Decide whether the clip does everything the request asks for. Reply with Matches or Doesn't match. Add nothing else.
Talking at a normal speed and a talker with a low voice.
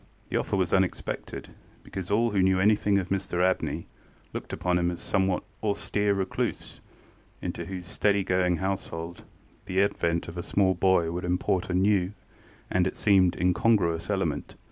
Matches